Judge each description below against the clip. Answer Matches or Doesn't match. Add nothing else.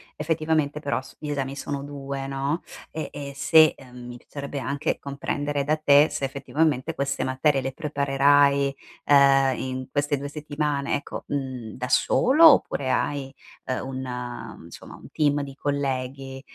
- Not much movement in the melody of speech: Matches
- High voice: Doesn't match